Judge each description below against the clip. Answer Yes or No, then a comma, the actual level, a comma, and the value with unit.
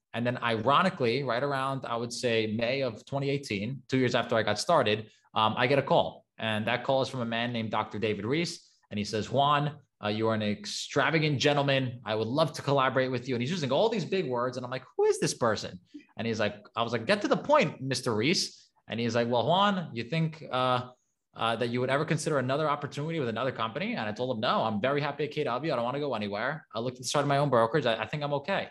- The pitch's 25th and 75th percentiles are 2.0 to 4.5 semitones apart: Yes, average, 4.0 semitones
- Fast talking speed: Yes, fast, 255 wpm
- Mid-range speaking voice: No, low, 130 Hz